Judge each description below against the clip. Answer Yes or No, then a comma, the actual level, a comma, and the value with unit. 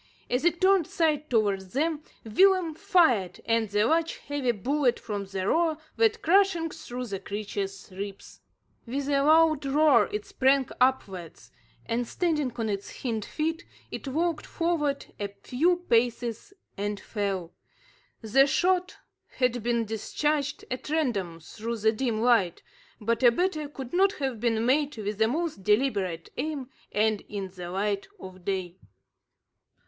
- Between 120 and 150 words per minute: Yes, average, 145 wpm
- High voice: Yes, high, 245 Hz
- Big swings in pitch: Yes, wide, 6.8 semitones